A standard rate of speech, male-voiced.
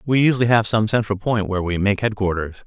No: fast, 225 wpm; male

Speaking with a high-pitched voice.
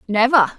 Yes: high, 230 Hz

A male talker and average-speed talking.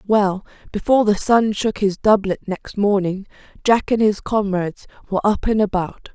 No: female; average, 165 wpm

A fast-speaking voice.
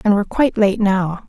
Yes: fast, 235 wpm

